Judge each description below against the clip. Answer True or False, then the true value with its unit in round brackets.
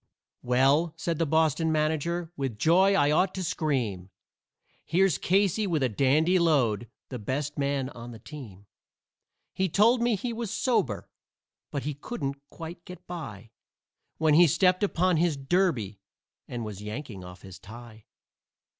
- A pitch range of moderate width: False (6.5 semitones)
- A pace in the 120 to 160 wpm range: True (150 wpm)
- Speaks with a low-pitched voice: False (150 Hz)